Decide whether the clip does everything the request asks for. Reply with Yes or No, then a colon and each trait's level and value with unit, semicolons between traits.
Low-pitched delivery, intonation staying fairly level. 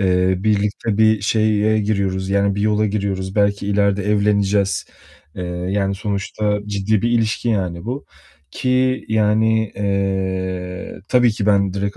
Yes: low, 100 Hz; narrow, 1.8 semitones